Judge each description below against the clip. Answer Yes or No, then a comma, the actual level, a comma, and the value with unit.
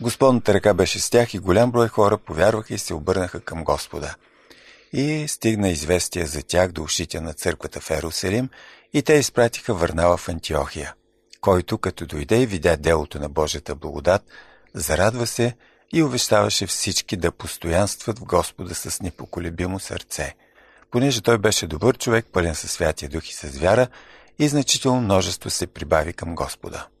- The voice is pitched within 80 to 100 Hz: Yes, very low, 95 Hz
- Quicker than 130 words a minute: Yes, average, 160 wpm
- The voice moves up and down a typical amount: No, wide, 6.2 semitones